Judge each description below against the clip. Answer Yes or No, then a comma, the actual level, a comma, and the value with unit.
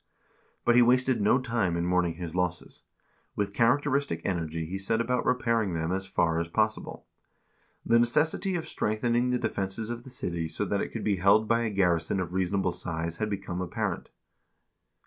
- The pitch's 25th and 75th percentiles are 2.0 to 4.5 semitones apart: No, average, 5.1 semitones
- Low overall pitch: Yes, low, 100 Hz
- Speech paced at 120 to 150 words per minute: No, average, 180 wpm